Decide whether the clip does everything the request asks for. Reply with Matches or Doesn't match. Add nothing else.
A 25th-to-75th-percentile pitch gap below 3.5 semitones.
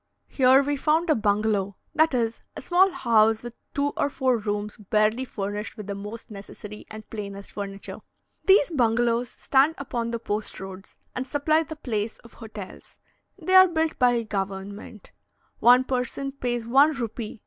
Doesn't match